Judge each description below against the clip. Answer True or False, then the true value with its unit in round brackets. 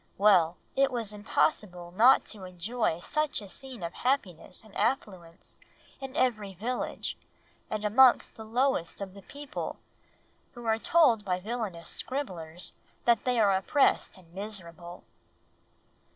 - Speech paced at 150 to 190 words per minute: False (135 wpm)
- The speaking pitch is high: True (210 Hz)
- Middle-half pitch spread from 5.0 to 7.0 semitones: True (5.5 semitones)